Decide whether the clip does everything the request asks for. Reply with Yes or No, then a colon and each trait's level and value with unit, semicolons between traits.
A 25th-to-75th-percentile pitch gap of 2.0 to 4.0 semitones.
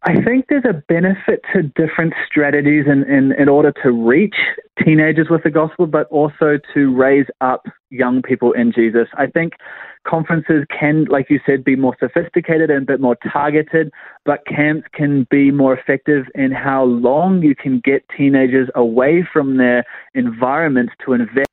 Yes: average, 3.5 semitones